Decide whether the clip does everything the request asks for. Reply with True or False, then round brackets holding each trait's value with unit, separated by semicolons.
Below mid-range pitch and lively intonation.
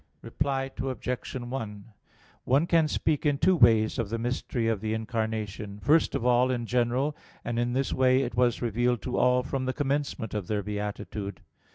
False (120 Hz; 3.2 semitones)